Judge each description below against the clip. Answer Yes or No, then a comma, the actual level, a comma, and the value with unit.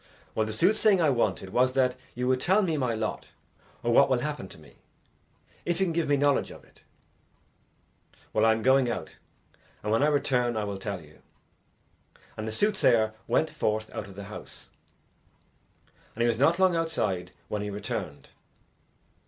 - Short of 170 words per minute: No, average, 180 wpm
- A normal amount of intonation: No, wide, 5.8 semitones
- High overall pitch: No, low, 120 Hz